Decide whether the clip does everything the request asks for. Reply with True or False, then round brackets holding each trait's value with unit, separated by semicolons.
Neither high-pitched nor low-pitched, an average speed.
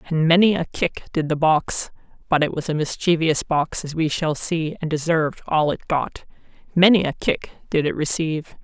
True (160 Hz; 180 wpm)